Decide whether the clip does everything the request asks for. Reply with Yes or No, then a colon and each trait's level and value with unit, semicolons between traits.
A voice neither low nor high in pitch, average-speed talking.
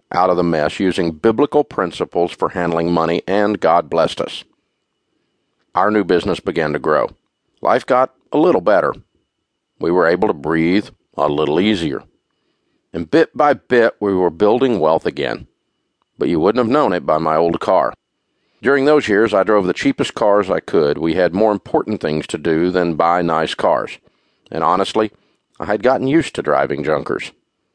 No: very low, 90 Hz; average, 175 wpm